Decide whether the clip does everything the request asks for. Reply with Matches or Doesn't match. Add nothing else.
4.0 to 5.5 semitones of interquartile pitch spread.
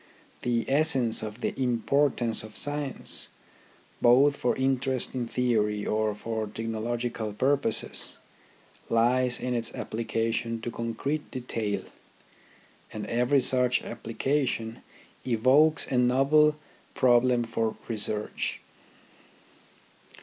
Doesn't match